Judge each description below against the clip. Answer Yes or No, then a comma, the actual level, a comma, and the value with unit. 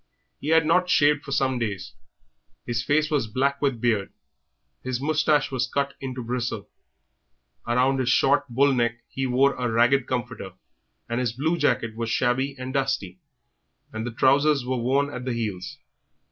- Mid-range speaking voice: No, low, 130 Hz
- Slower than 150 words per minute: No, average, 165 wpm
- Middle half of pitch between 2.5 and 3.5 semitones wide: Yes, average, 2.8 semitones